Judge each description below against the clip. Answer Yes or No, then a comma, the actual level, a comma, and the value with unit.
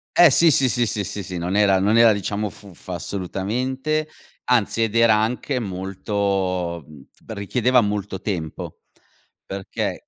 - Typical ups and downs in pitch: Yes, average, 3.6 semitones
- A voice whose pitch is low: Yes, low, 105 Hz